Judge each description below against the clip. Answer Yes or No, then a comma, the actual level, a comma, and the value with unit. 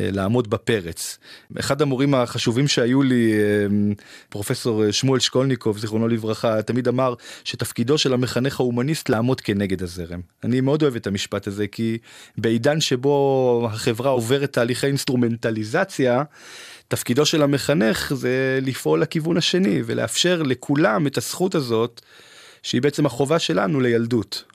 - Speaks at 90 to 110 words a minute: No, average, 125 wpm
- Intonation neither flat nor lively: Yes, average, 3.7 semitones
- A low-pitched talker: Yes, low, 125 Hz